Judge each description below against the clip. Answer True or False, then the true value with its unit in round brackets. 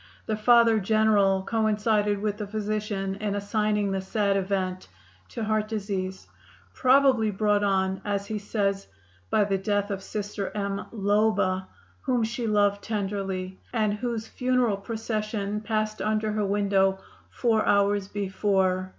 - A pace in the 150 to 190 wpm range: False (135 wpm)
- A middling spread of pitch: False (1.6 semitones)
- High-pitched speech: True (205 Hz)